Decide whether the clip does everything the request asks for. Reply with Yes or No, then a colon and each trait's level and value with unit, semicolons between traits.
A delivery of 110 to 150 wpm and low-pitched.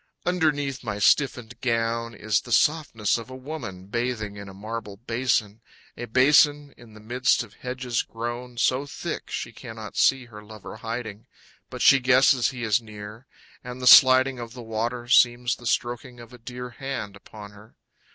No: average, 170 wpm; low, 120 Hz